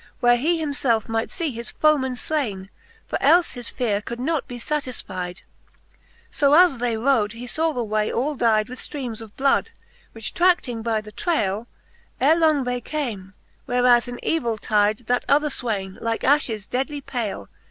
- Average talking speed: Yes, average, 175 wpm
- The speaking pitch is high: Yes, high, 245 Hz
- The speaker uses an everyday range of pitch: Yes, average, 4.6 semitones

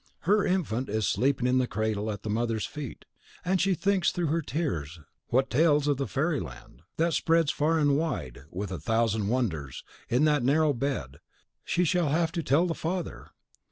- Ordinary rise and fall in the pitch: No, wide, 6.9 semitones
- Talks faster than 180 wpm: Yes, average, 190 wpm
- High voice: No, medium, 140 Hz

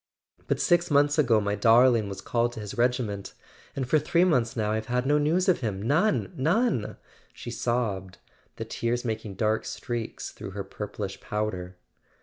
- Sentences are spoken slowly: No, average, 170 wpm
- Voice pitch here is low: Yes, low, 115 Hz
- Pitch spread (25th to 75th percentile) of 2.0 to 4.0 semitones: No, average, 4.9 semitones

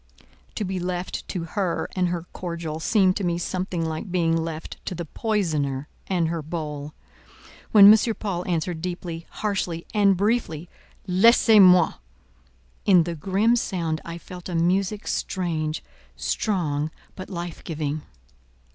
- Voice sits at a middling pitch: Yes, medium, 175 Hz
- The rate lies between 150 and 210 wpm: No, average, 140 wpm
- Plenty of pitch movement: No, average, 2.8 semitones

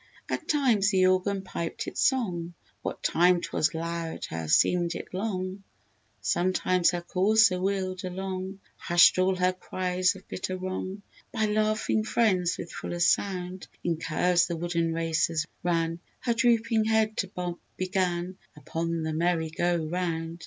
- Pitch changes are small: Yes, narrow, 2.1 semitones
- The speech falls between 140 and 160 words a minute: Yes, average, 145 wpm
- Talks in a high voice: No, medium, 180 Hz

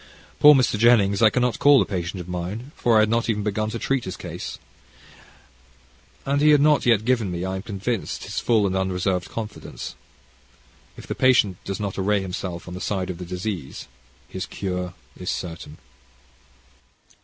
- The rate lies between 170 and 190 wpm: Yes, average, 180 wpm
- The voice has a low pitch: Yes, low, 100 Hz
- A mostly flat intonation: No, average, 4.1 semitones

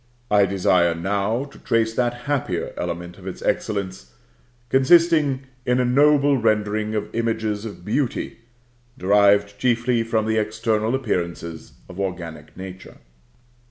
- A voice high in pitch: No, low, 110 Hz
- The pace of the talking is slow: Yes, slow, 125 wpm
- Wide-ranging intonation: No, average, 4.1 semitones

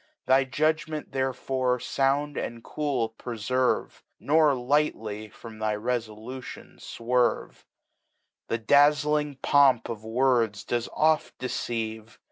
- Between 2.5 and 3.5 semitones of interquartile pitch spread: No, average, 3.9 semitones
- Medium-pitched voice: No, low, 125 Hz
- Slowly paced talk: Yes, slow, 100 wpm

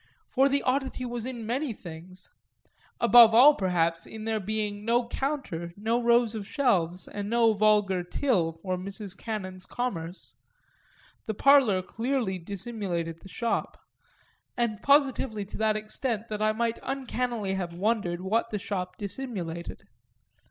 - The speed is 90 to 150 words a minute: Yes, average, 140 wpm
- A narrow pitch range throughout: No, average, 4.3 semitones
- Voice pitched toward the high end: Yes, high, 215 Hz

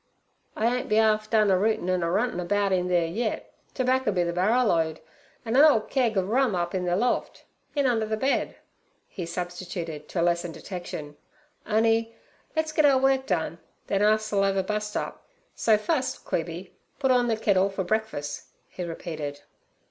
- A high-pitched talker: Yes, high, 205 Hz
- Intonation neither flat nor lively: Yes, average, 4.4 semitones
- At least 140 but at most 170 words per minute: No, average, 180 wpm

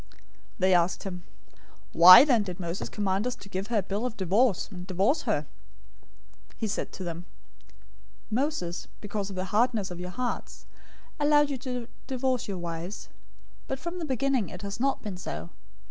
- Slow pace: No, average, 180 wpm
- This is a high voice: Yes, high, 200 Hz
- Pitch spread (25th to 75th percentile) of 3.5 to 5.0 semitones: No, wide, 5.6 semitones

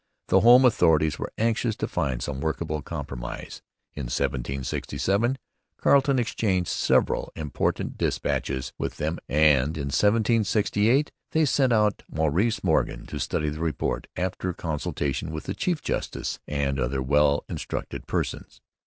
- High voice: No, very low, 80 Hz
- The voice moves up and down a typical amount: No, wide, 7.2 semitones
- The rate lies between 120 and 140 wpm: Yes, slow, 135 wpm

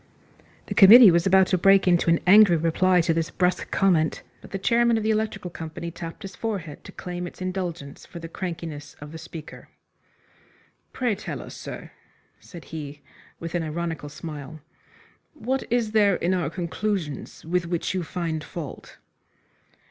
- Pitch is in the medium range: Yes, medium, 175 Hz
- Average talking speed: Yes, average, 165 wpm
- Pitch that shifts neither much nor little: Yes, average, 3.1 semitones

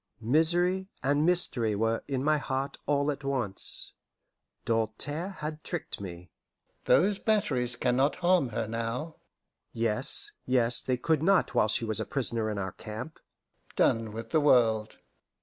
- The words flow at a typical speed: Yes, average, 150 wpm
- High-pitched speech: No, low, 130 Hz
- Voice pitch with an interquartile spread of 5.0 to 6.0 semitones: Yes, wide, 5.5 semitones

